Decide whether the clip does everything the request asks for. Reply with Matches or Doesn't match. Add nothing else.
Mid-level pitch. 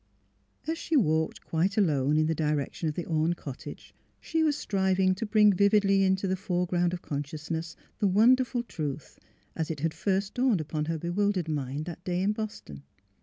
Matches